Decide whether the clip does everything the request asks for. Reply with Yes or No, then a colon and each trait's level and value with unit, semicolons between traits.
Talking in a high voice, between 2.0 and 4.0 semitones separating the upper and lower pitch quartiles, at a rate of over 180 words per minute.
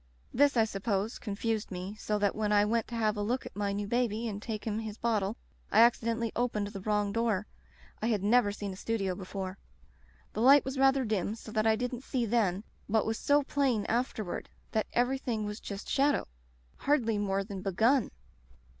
Yes: high, 220 Hz; narrow, 2.6 semitones; average, 200 wpm